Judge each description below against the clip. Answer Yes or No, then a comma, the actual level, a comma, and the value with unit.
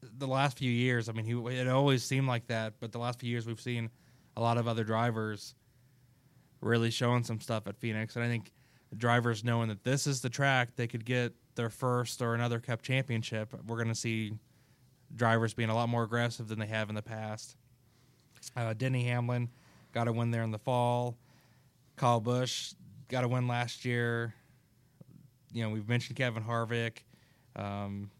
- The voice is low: Yes, low, 120 Hz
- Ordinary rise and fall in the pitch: No, narrow, 1.7 semitones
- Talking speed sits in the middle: Yes, average, 190 wpm